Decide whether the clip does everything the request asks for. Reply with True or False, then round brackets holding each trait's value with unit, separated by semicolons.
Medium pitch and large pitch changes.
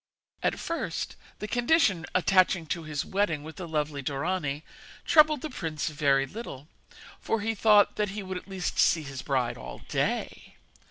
True (175 Hz; 5.8 semitones)